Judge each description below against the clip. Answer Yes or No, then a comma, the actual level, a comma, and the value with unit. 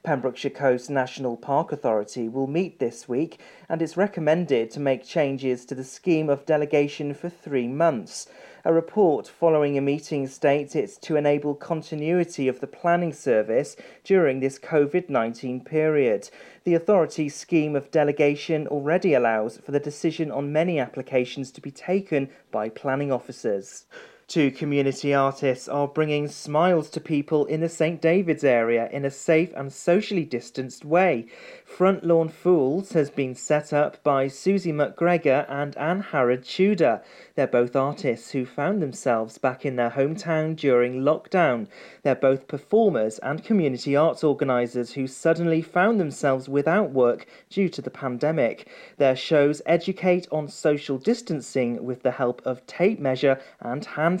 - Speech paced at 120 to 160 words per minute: Yes, average, 155 wpm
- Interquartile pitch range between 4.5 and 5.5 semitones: No, average, 3.8 semitones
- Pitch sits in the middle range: Yes, medium, 145 Hz